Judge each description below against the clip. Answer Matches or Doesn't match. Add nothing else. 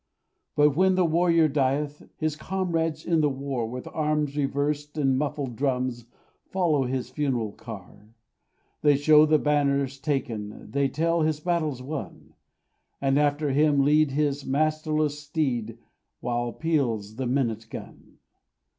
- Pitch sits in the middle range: Matches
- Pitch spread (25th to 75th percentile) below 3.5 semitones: Matches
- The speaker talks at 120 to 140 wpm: Matches